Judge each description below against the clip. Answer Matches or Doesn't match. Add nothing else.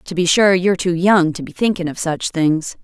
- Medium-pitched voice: Matches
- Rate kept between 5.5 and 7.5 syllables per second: Doesn't match